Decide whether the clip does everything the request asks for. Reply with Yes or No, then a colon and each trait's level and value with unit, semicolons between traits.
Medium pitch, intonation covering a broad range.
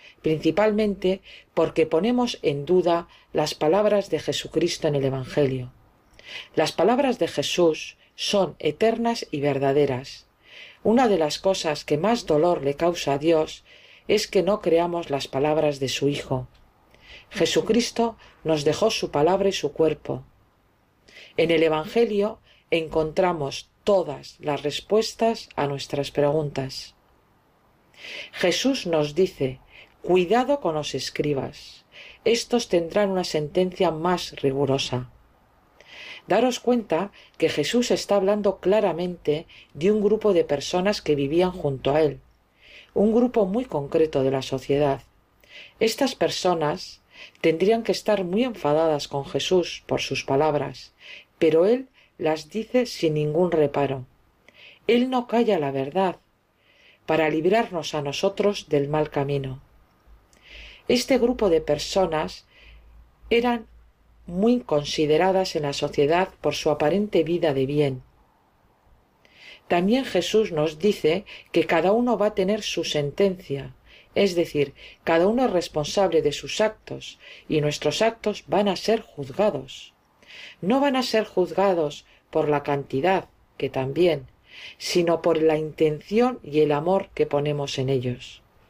Yes: medium, 160 Hz; wide, 5.7 semitones